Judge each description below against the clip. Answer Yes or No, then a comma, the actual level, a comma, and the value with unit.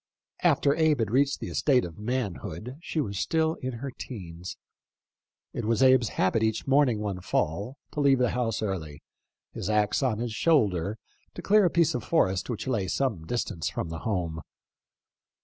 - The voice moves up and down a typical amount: No, wide, 5.7 semitones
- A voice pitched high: No, low, 115 Hz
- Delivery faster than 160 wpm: Yes, average, 170 wpm